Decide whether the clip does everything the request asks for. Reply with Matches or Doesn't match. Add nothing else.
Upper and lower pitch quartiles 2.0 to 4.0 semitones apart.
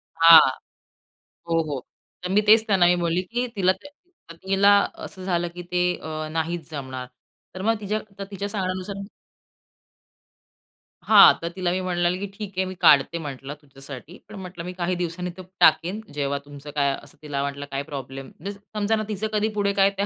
Doesn't match